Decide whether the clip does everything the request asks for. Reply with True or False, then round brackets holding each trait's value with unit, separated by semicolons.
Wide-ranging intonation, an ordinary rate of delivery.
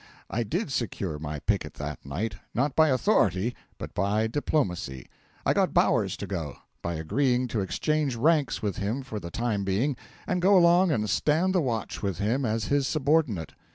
True (7.0 semitones; 180 wpm)